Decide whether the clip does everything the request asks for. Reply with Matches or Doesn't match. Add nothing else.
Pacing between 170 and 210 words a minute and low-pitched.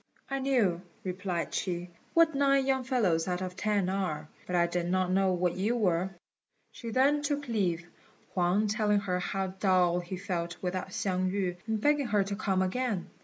Doesn't match